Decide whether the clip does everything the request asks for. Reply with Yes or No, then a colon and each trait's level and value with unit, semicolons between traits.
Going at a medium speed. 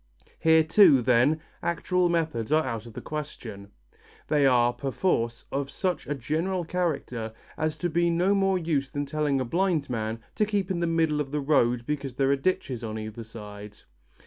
Yes: average, 185 wpm